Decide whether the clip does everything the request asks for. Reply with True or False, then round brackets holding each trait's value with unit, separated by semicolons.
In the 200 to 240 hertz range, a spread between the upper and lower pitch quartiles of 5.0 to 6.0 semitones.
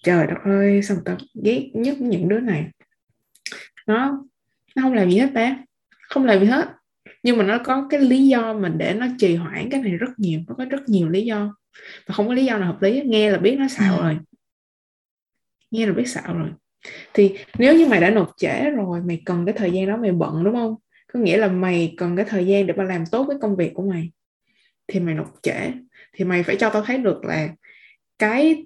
True (210 Hz; 5.3 semitones)